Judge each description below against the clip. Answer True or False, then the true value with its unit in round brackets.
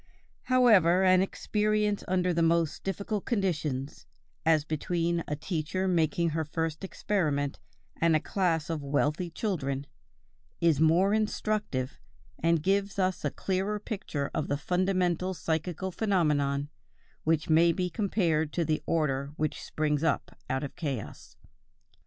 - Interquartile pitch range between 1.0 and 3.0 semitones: False (3.7 semitones)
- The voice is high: False (165 Hz)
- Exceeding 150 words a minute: False (135 wpm)